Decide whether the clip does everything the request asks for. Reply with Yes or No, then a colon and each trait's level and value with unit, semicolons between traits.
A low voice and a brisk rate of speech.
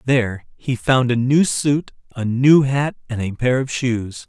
No: low, 125 Hz; average, 195 wpm